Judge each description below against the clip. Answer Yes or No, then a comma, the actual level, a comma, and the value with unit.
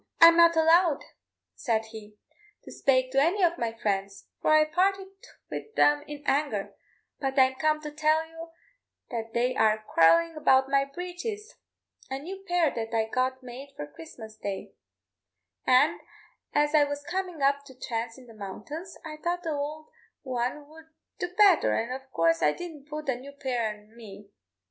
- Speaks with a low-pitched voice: No, very high, 280 Hz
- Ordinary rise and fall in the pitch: No, wide, 5.7 semitones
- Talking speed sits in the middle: Yes, average, 175 wpm